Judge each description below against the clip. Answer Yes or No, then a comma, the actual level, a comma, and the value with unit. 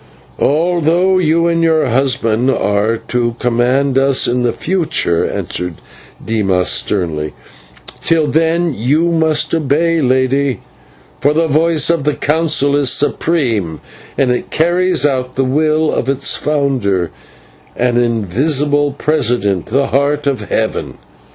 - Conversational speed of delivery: No, slow, 125 wpm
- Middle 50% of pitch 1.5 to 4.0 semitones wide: No, average, 4.6 semitones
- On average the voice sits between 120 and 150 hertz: Yes, medium, 140 Hz